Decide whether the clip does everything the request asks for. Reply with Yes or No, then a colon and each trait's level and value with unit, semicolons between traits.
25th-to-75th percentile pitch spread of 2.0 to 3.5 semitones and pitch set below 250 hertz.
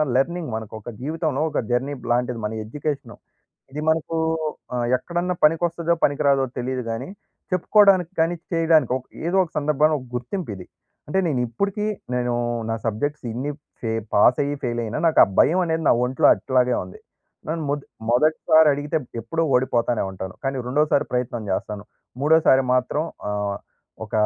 No: average, 4.8 semitones; medium, 140 Hz